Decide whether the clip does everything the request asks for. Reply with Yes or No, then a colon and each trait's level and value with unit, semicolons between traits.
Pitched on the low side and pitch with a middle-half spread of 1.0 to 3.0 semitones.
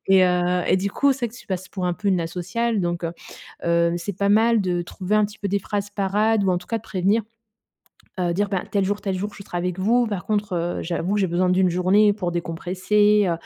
No: high, 190 Hz; average, 2.7 semitones